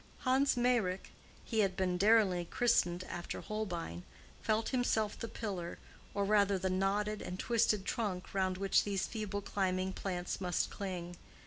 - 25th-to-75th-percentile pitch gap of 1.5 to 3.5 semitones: Yes, average, 2.9 semitones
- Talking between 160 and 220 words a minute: No, slow, 135 wpm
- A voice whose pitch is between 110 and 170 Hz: No, high, 195 Hz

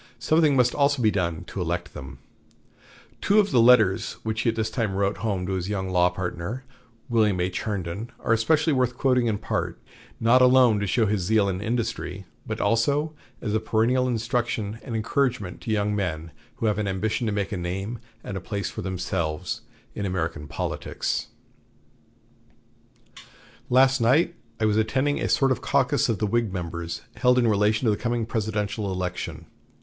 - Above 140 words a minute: Yes, average, 180 wpm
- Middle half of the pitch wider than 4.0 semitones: Yes, average, 4.4 semitones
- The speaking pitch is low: Yes, low, 110 Hz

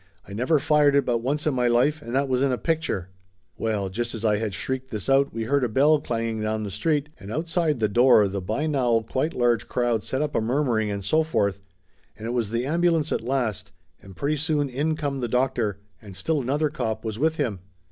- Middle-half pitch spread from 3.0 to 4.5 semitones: No, average, 5.0 semitones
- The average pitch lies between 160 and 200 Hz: No, low, 125 Hz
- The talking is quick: Yes, fast, 235 wpm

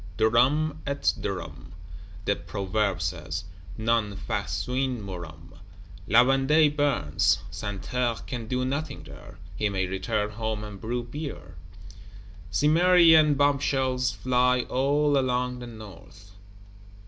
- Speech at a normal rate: No, slow, 110 wpm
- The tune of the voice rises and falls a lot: No, average, 5.0 semitones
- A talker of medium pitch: No, low, 125 Hz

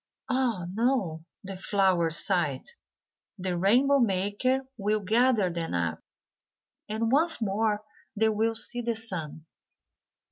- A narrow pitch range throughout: No, average, 4.3 semitones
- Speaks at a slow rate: Yes, slow, 115 wpm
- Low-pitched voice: No, high, 210 Hz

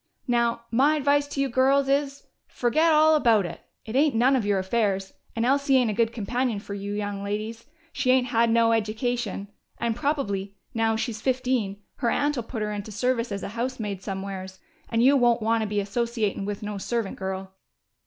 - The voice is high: Yes, high, 230 Hz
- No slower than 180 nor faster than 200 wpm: Yes, average, 195 wpm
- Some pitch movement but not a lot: Yes, average, 4.0 semitones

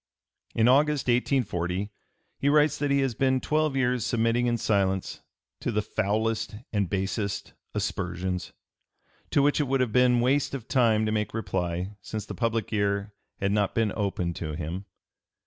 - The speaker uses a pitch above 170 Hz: No, low, 110 Hz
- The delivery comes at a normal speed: Yes, average, 165 wpm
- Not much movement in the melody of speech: No, average, 4.2 semitones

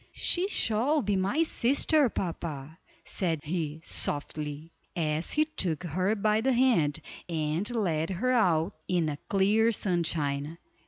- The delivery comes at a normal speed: No, slow, 130 wpm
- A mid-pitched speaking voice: Yes, medium, 180 Hz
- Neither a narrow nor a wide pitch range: No, wide, 6.1 semitones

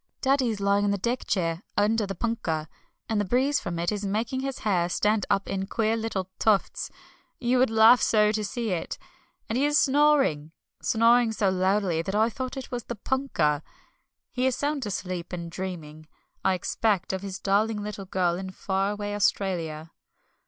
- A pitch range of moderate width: Yes, average, 3.8 semitones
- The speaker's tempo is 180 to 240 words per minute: Yes, average, 185 wpm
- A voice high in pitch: Yes, high, 205 Hz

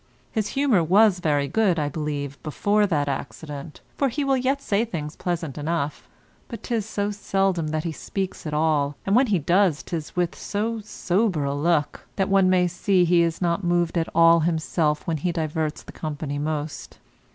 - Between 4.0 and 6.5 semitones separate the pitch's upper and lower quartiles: Yes, average, 4.6 semitones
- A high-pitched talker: No, medium, 170 Hz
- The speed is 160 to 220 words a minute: Yes, average, 185 wpm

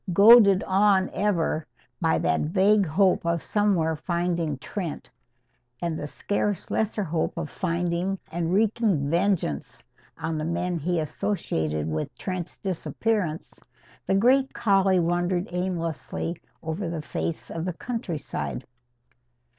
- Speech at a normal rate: No, slow, 125 wpm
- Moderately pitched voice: Yes, medium, 175 Hz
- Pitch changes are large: No, average, 3.5 semitones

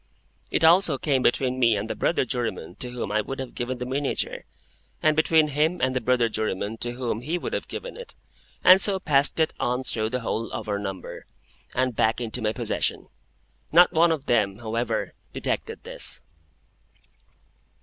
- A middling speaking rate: Yes, average, 180 wpm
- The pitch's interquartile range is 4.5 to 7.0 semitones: Yes, average, 5.2 semitones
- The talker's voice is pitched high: No, low, 125 Hz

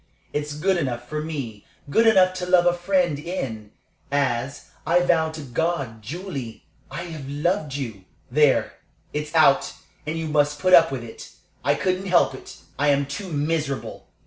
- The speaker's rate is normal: Yes, average, 170 wpm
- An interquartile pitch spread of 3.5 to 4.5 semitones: Yes, average, 4.1 semitones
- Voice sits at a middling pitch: Yes, medium, 150 Hz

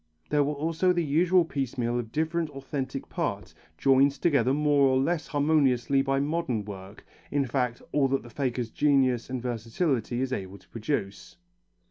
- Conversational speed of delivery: Yes, average, 160 wpm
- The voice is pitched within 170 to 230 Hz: No, low, 135 Hz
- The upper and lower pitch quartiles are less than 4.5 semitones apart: Yes, average, 3.4 semitones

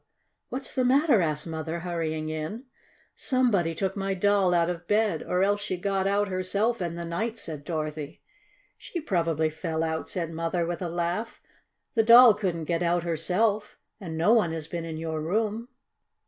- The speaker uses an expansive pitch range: No, average, 4.1 semitones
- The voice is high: No, medium, 175 Hz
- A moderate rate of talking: Yes, average, 175 wpm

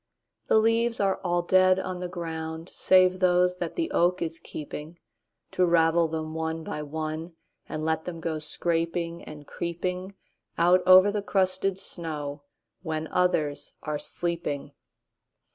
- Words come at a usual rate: No, slow, 125 wpm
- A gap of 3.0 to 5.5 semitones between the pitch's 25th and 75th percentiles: No, narrow, 2.4 semitones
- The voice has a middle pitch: Yes, medium, 170 Hz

